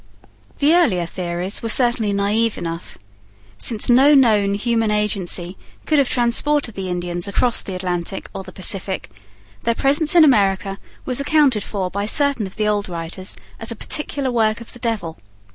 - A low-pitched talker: No, high, 210 Hz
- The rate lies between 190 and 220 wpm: No, average, 165 wpm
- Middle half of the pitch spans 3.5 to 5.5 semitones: Yes, average, 4.4 semitones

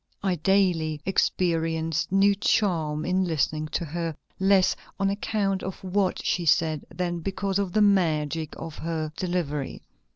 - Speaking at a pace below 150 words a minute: Yes, average, 140 wpm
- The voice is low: No, medium, 175 Hz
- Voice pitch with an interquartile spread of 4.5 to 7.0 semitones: No, average, 3.3 semitones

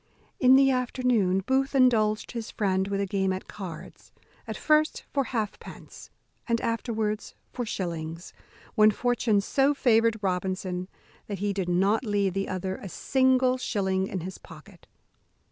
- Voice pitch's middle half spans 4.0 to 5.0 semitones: Yes, average, 4.6 semitones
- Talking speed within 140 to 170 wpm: Yes, average, 145 wpm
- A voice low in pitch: No, high, 210 Hz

